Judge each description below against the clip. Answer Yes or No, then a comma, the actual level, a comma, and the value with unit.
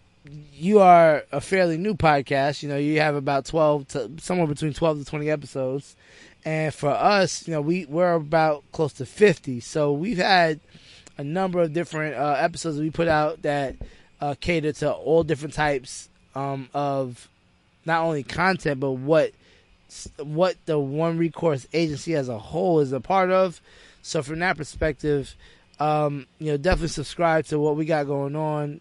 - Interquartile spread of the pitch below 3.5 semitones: Yes, narrow, 2.6 semitones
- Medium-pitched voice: Yes, medium, 150 Hz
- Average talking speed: Yes, average, 175 wpm